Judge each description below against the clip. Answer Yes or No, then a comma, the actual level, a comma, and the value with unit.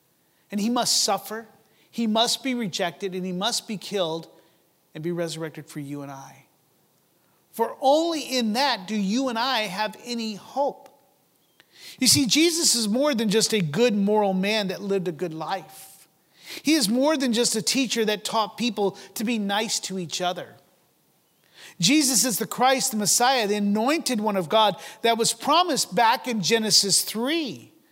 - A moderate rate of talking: Yes, average, 175 wpm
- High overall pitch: Yes, high, 215 Hz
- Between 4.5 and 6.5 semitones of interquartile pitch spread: No, average, 4.1 semitones